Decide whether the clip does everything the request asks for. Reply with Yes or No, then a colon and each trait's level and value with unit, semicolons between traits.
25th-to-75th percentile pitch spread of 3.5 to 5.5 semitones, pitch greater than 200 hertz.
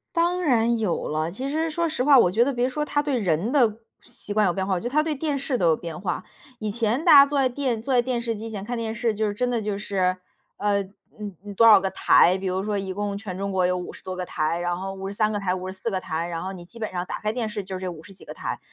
Yes: average, 4.6 semitones; high, 210 Hz